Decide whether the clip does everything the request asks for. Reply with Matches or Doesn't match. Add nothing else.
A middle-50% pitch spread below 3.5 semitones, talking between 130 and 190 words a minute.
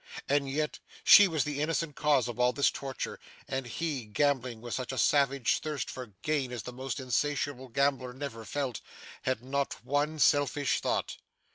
Matches